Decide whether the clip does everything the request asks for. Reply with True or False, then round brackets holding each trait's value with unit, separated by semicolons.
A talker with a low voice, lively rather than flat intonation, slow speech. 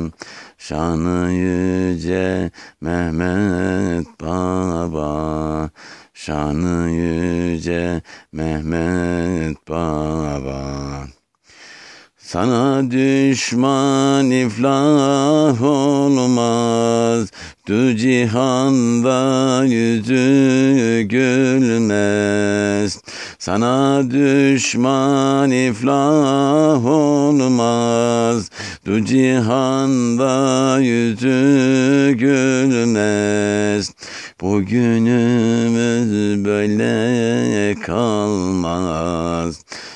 True (115 Hz; 6.7 semitones; 40 wpm)